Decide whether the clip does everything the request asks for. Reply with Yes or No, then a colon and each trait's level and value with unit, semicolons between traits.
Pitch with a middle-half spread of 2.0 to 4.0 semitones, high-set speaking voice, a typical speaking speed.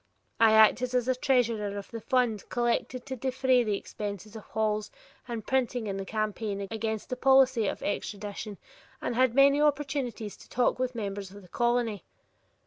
Yes: average, 3.3 semitones; high, 230 Hz; average, 165 wpm